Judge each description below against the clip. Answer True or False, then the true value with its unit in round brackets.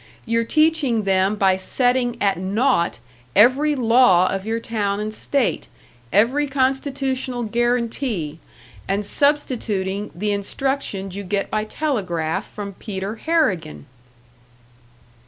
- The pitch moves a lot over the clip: False (4.9 semitones)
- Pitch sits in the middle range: False (220 Hz)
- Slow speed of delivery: True (110 wpm)